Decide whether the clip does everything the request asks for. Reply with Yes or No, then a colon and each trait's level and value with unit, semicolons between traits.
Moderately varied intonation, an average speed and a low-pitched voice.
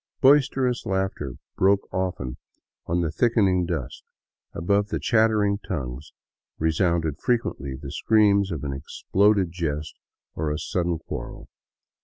No: average, 5.0 semitones; slow, 120 wpm; very low, 90 Hz